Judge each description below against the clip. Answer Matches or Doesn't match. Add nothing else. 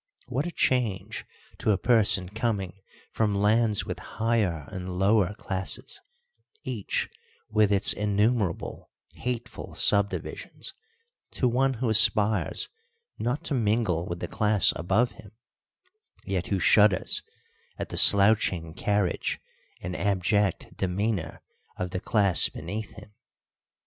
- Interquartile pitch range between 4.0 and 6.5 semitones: Doesn't match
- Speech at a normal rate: Doesn't match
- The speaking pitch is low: Matches